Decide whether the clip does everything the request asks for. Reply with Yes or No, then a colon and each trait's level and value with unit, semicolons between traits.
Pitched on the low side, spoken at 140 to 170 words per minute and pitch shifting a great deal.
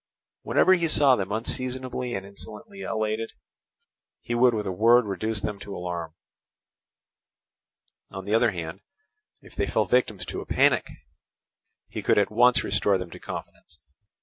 No: low, 110 Hz; average, 150 wpm; average, 4.1 semitones